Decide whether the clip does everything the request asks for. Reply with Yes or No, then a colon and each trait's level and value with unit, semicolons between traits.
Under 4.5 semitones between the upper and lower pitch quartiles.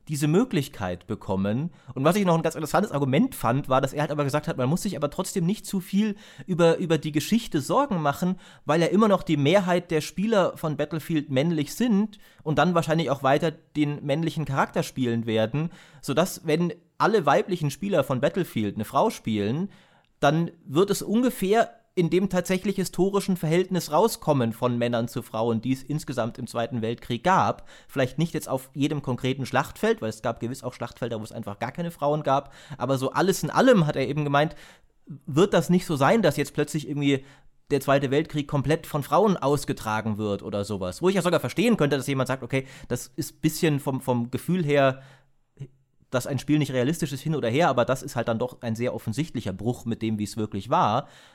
No: average, 5.0 semitones